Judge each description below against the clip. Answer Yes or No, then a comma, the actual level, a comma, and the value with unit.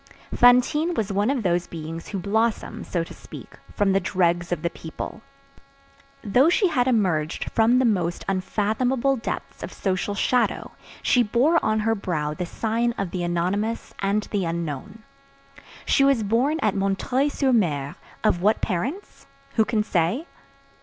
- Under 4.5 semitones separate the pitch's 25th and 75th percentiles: No, average, 5.3 semitones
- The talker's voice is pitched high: Yes, high, 210 Hz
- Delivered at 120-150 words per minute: No, average, 160 wpm